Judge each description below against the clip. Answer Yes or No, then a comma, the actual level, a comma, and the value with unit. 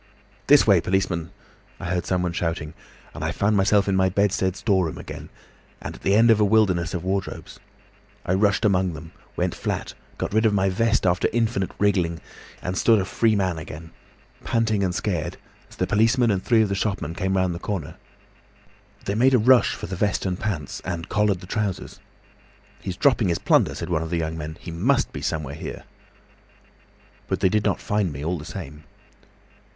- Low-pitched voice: Yes, very low, 95 Hz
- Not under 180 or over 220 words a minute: Yes, average, 195 wpm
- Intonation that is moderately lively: Yes, average, 3.6 semitones